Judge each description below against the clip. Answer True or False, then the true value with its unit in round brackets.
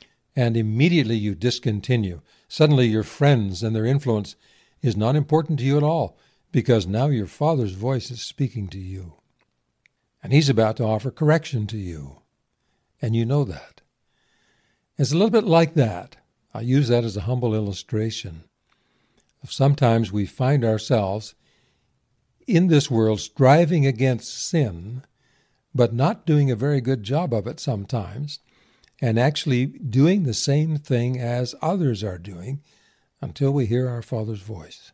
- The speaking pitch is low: True (125 Hz)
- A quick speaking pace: False (150 wpm)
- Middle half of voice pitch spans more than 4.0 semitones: True (4.5 semitones)